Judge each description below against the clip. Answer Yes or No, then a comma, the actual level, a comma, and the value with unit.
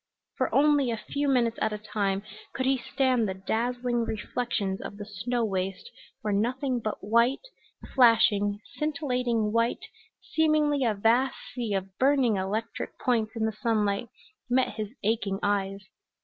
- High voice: Yes, high, 230 Hz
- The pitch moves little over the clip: No, average, 3.6 semitones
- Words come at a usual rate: Yes, average, 150 wpm